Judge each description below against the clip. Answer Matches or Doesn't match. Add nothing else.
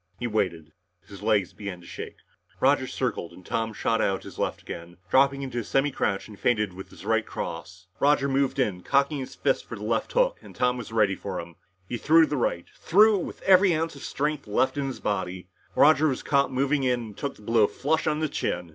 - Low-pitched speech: Matches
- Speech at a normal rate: Doesn't match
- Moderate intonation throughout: Doesn't match